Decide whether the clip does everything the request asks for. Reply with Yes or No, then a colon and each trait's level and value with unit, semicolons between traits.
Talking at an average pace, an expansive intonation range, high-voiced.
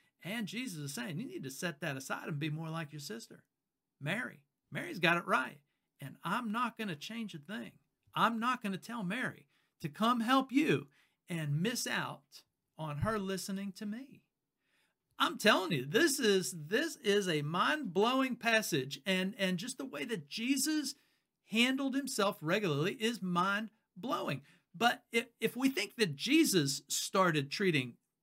Yes: average, 165 wpm; wide, 6.1 semitones; high, 200 Hz